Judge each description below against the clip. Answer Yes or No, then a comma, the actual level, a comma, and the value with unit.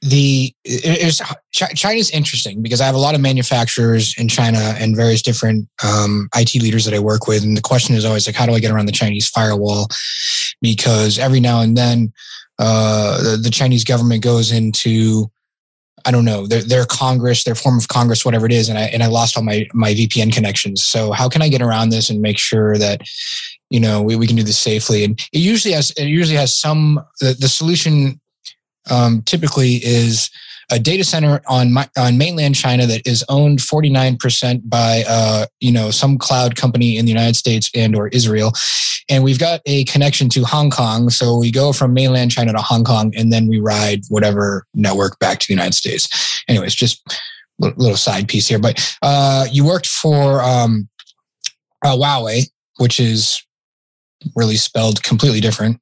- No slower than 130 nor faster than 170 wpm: No, average, 195 wpm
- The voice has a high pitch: No, low, 120 Hz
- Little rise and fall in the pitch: No, average, 3.3 semitones